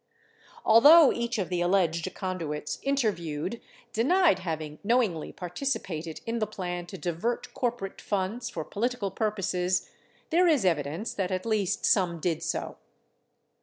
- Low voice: No, high, 190 Hz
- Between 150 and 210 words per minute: No, slow, 135 wpm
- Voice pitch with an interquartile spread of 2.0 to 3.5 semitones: No, average, 5.2 semitones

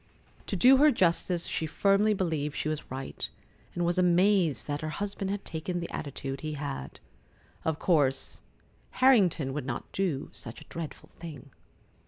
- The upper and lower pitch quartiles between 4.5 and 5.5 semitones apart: Yes, average, 4.8 semitones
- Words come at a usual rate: Yes, average, 160 wpm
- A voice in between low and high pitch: Yes, medium, 165 Hz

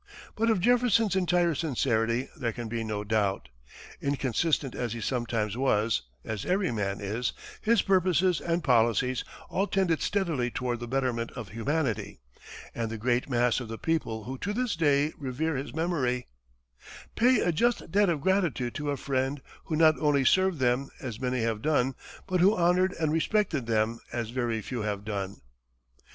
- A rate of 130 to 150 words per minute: No, average, 170 wpm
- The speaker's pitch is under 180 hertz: Yes, low, 135 Hz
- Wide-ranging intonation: Yes, wide, 6.6 semitones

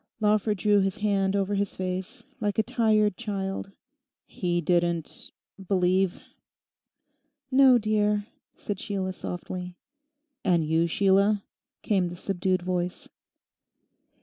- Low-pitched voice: No, high, 195 Hz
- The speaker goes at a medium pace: No, slow, 105 wpm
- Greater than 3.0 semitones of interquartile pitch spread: No, narrow, 2.5 semitones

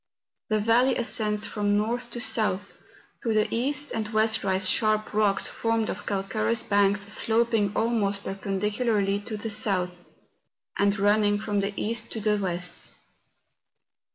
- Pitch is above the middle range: Yes, high, 210 Hz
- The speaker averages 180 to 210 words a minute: No, average, 140 wpm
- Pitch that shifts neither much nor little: No, narrow, 2.0 semitones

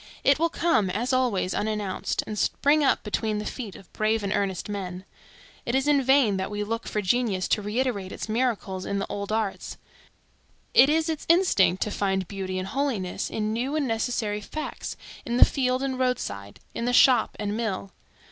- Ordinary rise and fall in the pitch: Yes, average, 4.6 semitones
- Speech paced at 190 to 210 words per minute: Yes, average, 195 wpm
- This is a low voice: No, high, 215 Hz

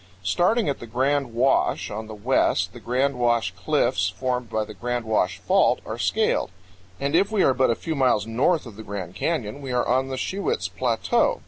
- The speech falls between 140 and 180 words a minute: No, fast, 205 wpm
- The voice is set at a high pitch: No, low, 125 Hz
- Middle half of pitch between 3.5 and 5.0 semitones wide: Yes, average, 4.1 semitones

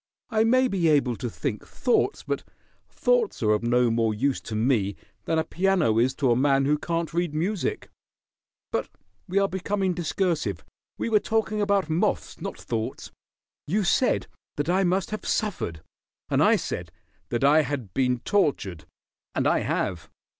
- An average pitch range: No, wide, 8.4 semitones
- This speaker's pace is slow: No, average, 170 wpm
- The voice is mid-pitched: Yes, medium, 155 Hz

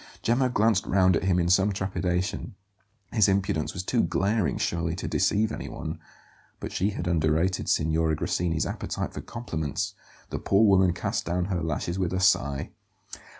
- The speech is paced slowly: No, average, 160 wpm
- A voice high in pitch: No, very low, 90 Hz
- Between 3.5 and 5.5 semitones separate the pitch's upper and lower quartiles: No, average, 3.0 semitones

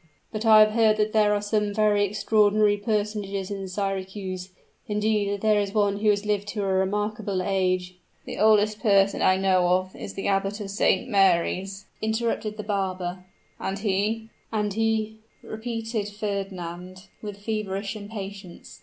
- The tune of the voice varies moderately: No, narrow, 1.8 semitones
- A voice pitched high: Yes, high, 205 Hz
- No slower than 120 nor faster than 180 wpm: Yes, average, 165 wpm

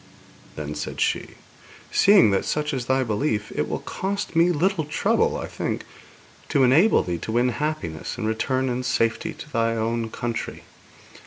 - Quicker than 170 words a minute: No, average, 165 wpm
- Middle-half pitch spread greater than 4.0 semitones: Yes, average, 5.2 semitones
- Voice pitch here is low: Yes, low, 125 Hz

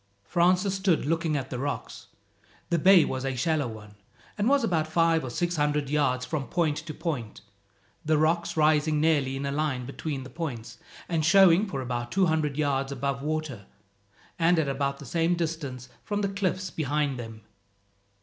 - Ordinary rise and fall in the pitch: Yes, average, 3.7 semitones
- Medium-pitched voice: Yes, medium, 155 Hz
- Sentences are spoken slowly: No, average, 180 wpm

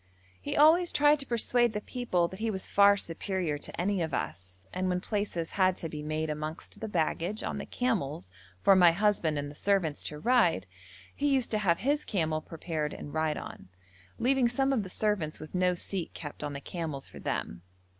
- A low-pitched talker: No, medium, 180 Hz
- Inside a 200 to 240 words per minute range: Yes, fast, 205 wpm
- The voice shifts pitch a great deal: Yes, wide, 5.7 semitones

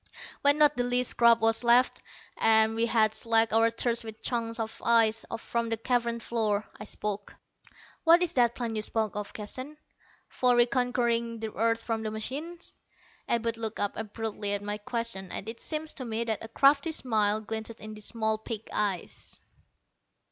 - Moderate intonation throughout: No, narrow, 1.7 semitones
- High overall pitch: Yes, high, 230 Hz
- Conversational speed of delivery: Yes, average, 175 wpm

